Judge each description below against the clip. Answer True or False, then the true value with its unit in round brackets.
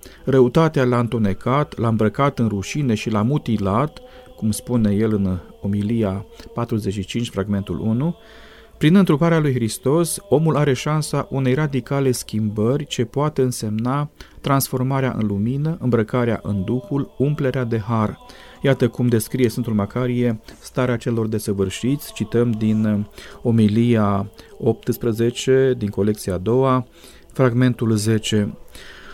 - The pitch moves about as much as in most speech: True (3.7 semitones)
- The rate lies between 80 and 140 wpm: True (120 wpm)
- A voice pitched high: False (120 Hz)